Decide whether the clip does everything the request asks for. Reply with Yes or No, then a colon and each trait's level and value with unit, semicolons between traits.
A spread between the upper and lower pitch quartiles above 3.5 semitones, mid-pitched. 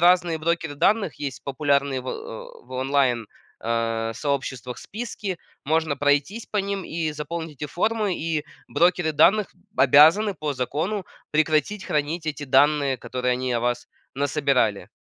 Yes: average, 4.6 semitones; medium, 150 Hz